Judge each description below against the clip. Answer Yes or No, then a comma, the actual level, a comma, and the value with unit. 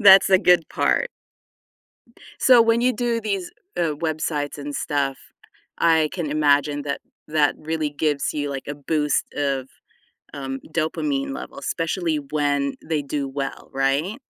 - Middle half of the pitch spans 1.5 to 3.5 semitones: No, average, 3.9 semitones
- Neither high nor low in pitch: Yes, medium, 150 Hz